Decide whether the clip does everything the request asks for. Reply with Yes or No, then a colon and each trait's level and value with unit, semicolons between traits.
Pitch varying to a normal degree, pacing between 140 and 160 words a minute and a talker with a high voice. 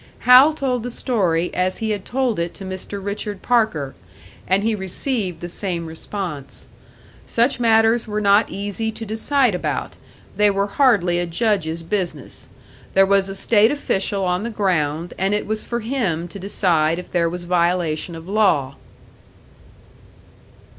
Yes: average, 4.1 semitones; average, 155 wpm; high, 195 Hz